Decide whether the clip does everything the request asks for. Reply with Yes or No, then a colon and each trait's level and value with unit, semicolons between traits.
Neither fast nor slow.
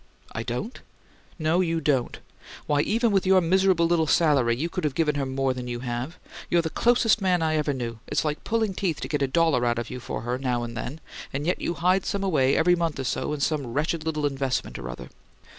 No: fast, 235 wpm